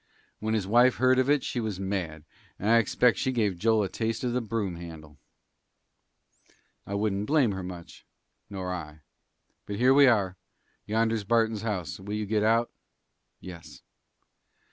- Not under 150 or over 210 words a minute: Yes, average, 165 wpm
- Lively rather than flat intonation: No, average, 3.6 semitones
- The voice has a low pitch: Yes, low, 105 Hz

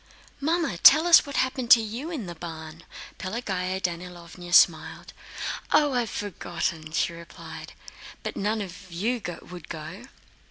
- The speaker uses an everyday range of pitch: No, wide, 6.1 semitones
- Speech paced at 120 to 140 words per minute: Yes, slow, 135 wpm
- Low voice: No, medium, 185 Hz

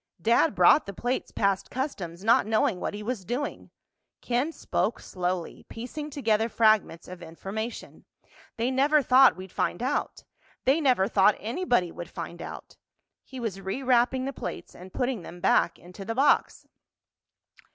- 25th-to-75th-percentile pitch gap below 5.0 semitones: No, wide, 5.6 semitones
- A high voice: Yes, high, 225 Hz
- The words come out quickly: No, average, 150 wpm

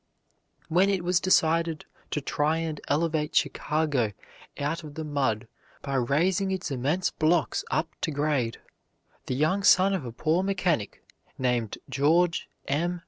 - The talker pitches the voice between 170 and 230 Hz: No, medium, 155 Hz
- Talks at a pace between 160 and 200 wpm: No, average, 140 wpm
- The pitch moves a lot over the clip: No, average, 3.8 semitones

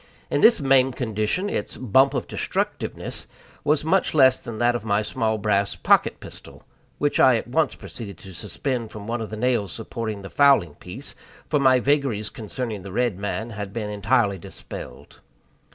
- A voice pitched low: Yes, low, 115 Hz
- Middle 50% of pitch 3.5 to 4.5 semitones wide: Yes, average, 4.2 semitones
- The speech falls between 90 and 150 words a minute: No, average, 175 wpm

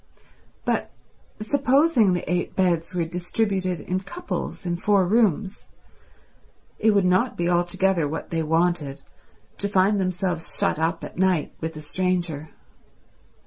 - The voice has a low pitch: No, medium, 180 Hz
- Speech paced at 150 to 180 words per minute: No, slow, 135 wpm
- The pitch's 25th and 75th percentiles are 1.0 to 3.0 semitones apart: Yes, average, 2.7 semitones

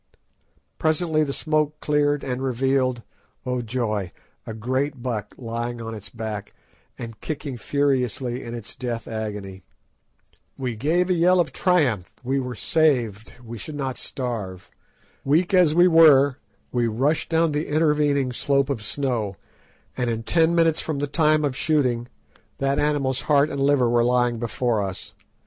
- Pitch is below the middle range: Yes, low, 130 Hz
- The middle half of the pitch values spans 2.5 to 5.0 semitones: Yes, average, 4.2 semitones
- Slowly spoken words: No, average, 145 wpm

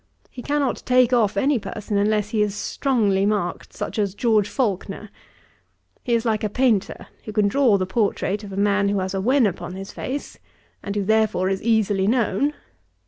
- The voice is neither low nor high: No, high, 210 Hz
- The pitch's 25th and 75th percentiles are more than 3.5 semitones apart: No, average, 3.0 semitones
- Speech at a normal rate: Yes, average, 190 wpm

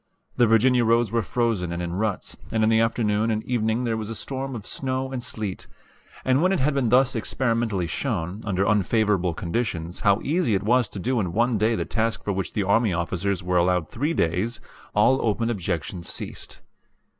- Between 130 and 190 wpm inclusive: No, average, 200 wpm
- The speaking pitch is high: No, low, 110 Hz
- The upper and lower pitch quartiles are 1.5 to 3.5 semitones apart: No, average, 4.0 semitones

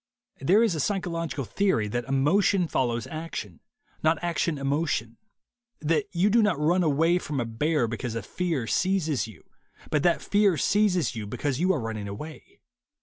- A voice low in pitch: No, medium, 155 Hz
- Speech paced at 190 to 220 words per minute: No, average, 170 wpm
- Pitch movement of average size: No, wide, 6.6 semitones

